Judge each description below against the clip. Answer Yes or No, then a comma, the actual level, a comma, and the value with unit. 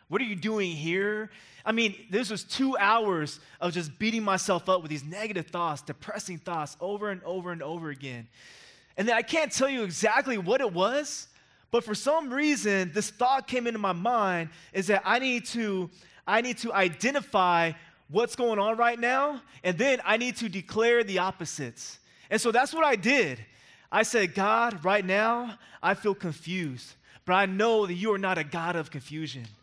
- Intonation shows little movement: No, average, 5.0 semitones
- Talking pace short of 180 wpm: No, average, 190 wpm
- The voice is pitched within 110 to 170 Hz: No, high, 200 Hz